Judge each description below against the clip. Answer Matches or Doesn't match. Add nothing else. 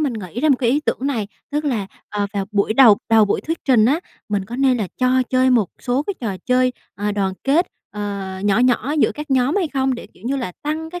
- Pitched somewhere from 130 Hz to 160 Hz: Doesn't match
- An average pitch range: Matches